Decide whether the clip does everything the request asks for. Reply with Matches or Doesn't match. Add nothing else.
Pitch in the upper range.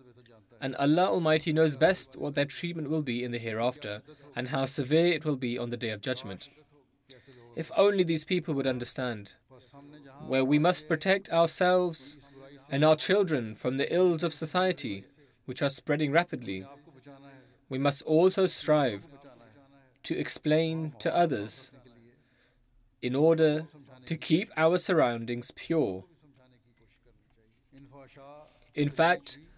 Doesn't match